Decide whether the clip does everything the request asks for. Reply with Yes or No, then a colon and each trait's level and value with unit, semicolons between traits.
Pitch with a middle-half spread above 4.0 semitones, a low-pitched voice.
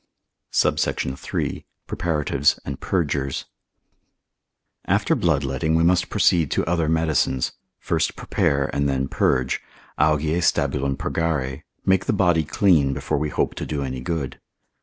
No: average, 3.2 semitones; very low, 75 Hz